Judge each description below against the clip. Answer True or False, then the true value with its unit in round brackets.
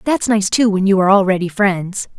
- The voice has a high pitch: True (200 Hz)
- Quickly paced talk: True (220 wpm)